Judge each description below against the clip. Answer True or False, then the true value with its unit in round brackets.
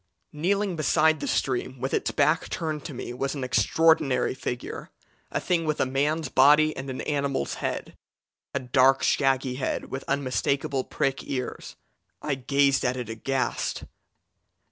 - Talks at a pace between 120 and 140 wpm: False (150 wpm)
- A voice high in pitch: False (135 Hz)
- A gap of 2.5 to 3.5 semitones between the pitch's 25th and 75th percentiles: True (2.8 semitones)